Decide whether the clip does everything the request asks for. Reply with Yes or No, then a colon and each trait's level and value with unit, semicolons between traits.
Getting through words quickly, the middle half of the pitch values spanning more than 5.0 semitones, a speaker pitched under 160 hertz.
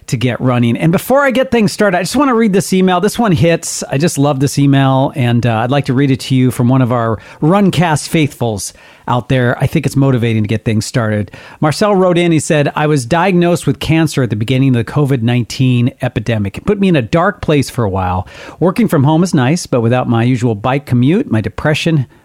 Yes: fast, 245 wpm; wide, 5.4 semitones; medium, 140 Hz